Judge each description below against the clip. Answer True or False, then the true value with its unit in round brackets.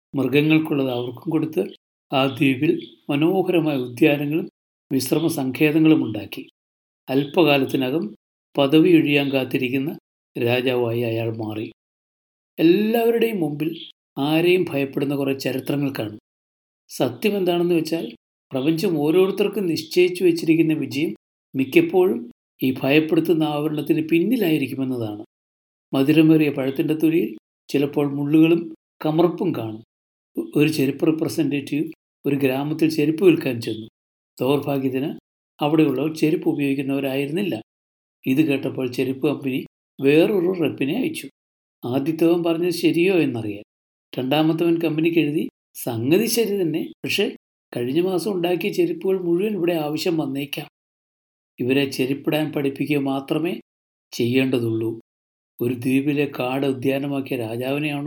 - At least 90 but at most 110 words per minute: True (95 wpm)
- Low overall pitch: False (145 Hz)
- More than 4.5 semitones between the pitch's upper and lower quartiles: False (3.7 semitones)